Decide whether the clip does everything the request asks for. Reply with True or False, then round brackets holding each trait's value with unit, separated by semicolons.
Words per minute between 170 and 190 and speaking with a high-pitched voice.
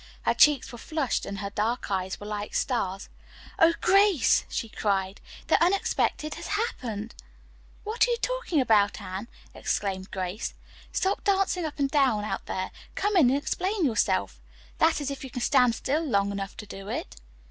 True (180 wpm; 245 Hz)